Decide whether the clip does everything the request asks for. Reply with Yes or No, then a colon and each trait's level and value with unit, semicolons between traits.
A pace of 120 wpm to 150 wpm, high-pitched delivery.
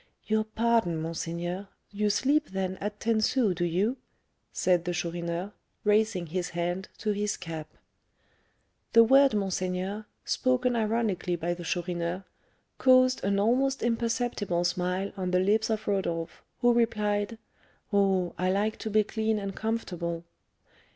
Yes: slow, 135 wpm; high, 200 Hz